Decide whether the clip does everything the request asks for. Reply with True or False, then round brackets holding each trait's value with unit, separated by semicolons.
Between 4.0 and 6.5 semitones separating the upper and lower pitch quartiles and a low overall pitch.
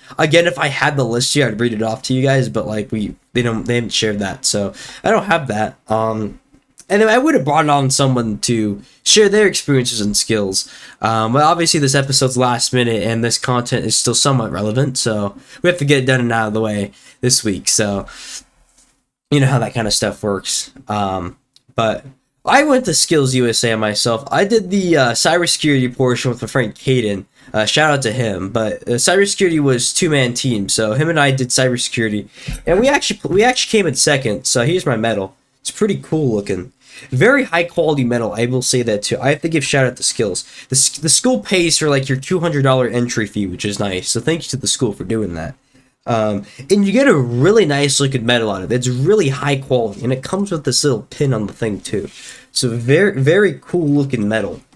True (4.5 semitones; 130 Hz)